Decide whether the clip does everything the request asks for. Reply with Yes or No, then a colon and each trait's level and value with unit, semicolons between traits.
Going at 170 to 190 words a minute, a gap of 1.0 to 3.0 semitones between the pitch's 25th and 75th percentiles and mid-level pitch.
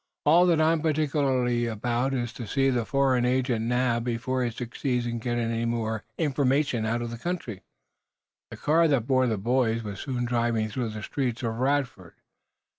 No: average, 175 wpm; average, 2.7 semitones; low, 125 Hz